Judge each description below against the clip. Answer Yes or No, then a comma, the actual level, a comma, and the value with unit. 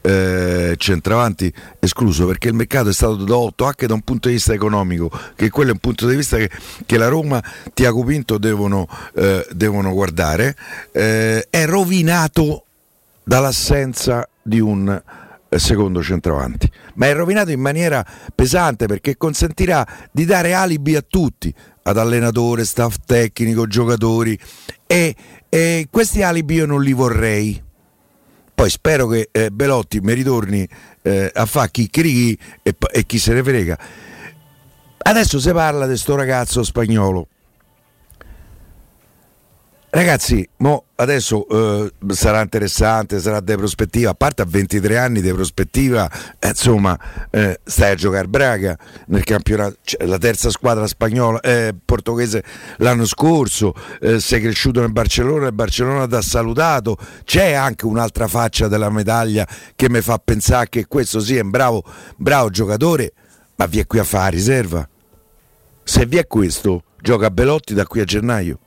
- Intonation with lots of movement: No, average, 4.2 semitones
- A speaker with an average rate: Yes, average, 150 wpm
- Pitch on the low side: Yes, low, 115 Hz